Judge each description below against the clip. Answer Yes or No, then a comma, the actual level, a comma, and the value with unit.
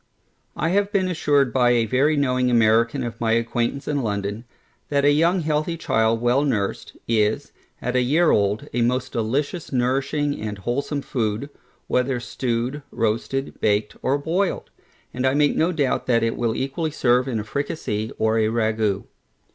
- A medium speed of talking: Yes, average, 170 wpm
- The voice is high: No, low, 125 Hz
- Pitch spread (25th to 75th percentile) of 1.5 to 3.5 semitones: No, average, 4.1 semitones